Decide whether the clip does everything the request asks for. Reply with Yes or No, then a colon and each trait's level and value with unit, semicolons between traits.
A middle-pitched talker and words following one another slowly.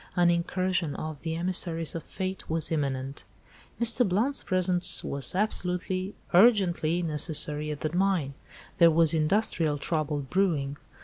Yes: medium, 170 Hz; slow, 130 wpm